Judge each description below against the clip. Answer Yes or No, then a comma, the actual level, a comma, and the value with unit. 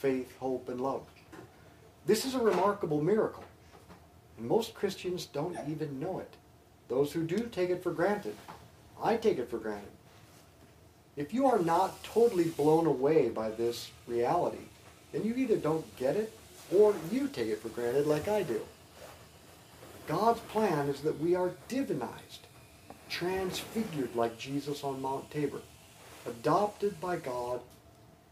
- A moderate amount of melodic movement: No, wide, 8.8 semitones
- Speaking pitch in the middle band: Yes, medium, 155 Hz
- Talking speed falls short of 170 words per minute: Yes, average, 145 wpm